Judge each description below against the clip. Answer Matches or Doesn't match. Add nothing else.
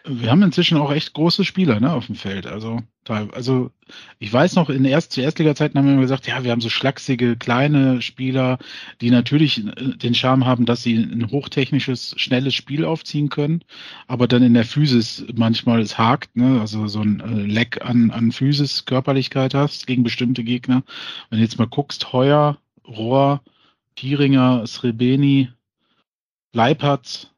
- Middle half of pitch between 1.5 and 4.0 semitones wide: Matches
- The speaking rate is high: Doesn't match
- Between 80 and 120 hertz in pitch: Doesn't match